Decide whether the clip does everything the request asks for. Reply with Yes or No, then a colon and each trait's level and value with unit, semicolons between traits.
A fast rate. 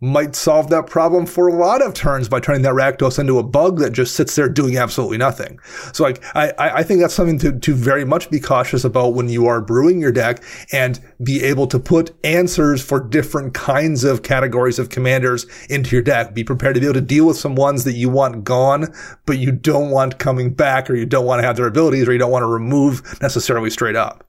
Yes: fast, 235 wpm